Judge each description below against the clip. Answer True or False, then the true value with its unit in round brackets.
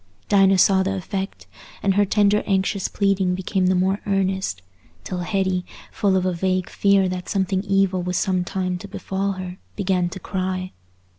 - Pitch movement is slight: True (1.1 semitones)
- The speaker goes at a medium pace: True (170 wpm)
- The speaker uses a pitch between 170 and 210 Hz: True (190 Hz)